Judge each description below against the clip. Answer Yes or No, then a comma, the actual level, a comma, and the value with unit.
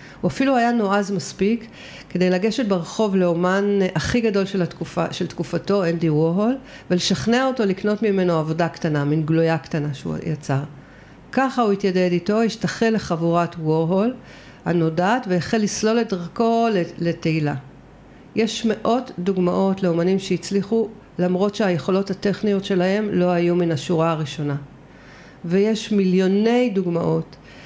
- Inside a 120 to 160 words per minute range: Yes, average, 125 wpm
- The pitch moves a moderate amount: Yes, average, 3.9 semitones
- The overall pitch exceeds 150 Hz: Yes, medium, 185 Hz